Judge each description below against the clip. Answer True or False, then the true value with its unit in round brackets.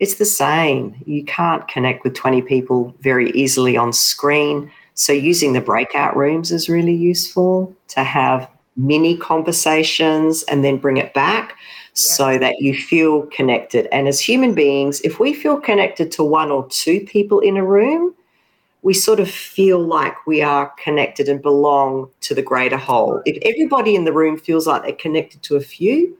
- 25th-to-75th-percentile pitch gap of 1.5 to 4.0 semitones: False (4.8 semitones)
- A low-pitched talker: False (155 Hz)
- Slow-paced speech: False (175 wpm)